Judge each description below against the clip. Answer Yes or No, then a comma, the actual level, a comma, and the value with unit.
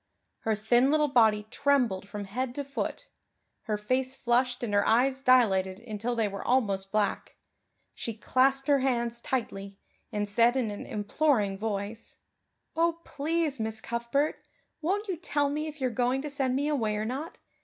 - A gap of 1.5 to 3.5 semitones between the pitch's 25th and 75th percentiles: No, average, 4.6 semitones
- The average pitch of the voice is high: Yes, high, 245 Hz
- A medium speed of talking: Yes, average, 170 wpm